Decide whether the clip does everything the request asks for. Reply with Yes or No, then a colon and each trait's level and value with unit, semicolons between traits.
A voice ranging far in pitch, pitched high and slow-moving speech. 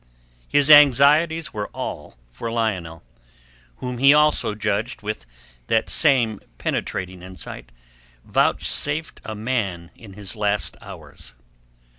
No: wide, 6.1 semitones; low, 110 Hz; slow, 110 wpm